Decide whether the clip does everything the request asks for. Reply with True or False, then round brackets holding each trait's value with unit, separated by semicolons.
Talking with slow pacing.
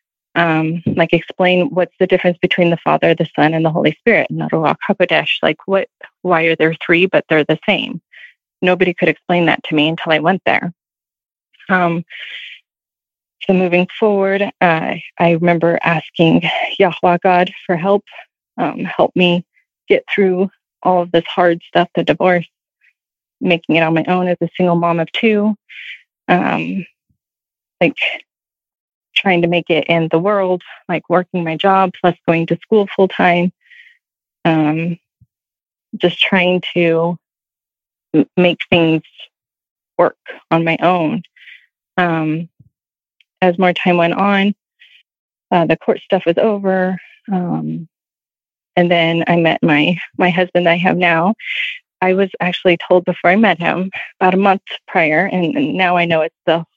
False (155 wpm)